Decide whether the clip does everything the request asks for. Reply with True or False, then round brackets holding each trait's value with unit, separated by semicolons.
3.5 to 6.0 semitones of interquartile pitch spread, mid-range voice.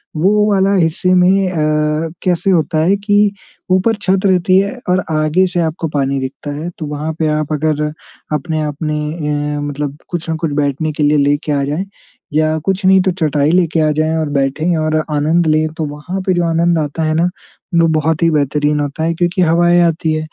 False (2.9 semitones; 160 Hz)